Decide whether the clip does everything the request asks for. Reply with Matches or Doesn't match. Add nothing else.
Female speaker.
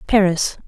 Matches